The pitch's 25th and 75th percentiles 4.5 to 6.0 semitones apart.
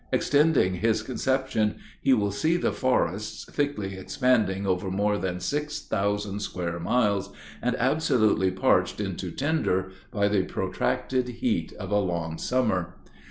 Yes: average, 5.2 semitones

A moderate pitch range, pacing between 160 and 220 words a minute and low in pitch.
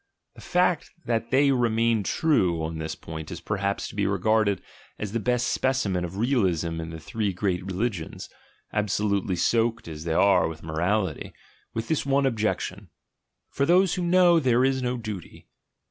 No: wide, 5.7 semitones; average, 165 wpm; low, 105 Hz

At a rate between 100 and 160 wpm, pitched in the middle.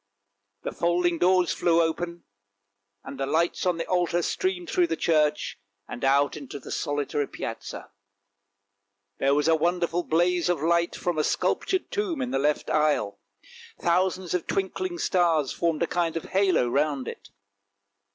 Yes: average, 155 wpm; medium, 170 Hz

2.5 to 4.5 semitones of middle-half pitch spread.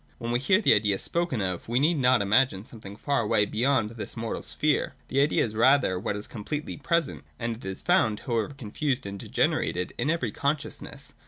No: average, 5.2 semitones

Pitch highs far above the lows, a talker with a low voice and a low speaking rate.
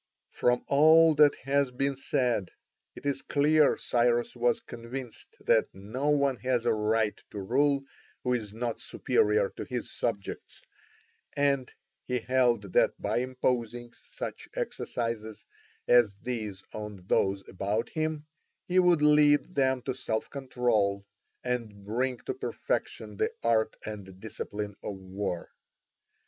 No: average, 4.3 semitones; low, 120 Hz; slow, 130 wpm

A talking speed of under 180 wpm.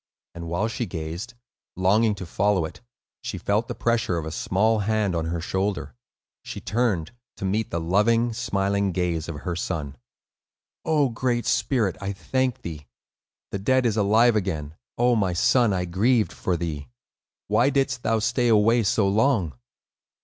Yes: average, 165 wpm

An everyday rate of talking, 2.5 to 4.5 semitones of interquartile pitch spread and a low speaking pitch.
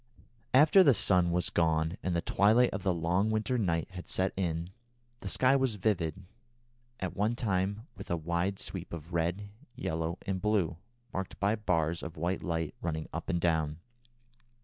Yes: average, 170 wpm; average, 3.6 semitones; very low, 90 Hz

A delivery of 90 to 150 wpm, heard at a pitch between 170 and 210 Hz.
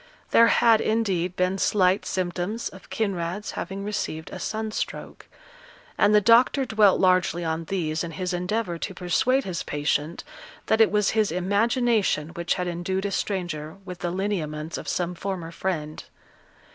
No: average, 160 wpm; medium, 185 Hz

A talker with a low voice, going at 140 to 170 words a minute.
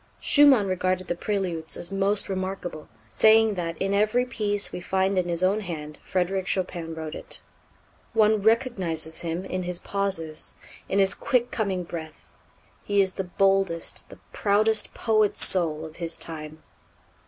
No: high, 190 Hz; average, 155 wpm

